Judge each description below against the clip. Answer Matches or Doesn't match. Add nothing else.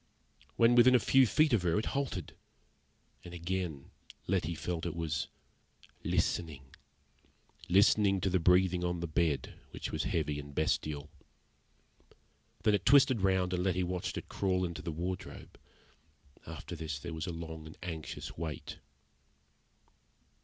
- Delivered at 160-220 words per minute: Doesn't match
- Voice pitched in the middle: Doesn't match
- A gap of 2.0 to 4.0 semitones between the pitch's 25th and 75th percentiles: Matches